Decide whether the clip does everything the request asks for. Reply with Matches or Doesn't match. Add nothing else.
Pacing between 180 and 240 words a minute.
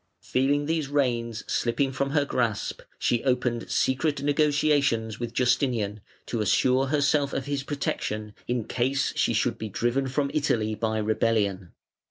Doesn't match